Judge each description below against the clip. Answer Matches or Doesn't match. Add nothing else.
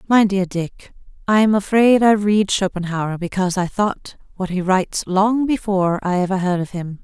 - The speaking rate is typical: Matches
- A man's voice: Doesn't match